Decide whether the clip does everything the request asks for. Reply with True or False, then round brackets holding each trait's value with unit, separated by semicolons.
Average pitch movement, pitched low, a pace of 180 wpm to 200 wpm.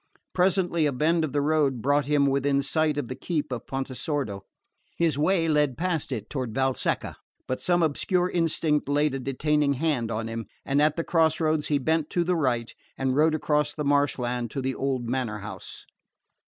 False (3.2 semitones; 145 Hz; 190 wpm)